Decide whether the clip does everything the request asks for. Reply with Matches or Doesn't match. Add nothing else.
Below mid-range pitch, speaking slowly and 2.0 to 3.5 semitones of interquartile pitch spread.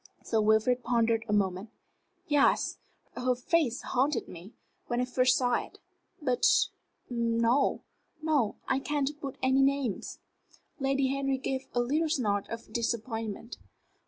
Doesn't match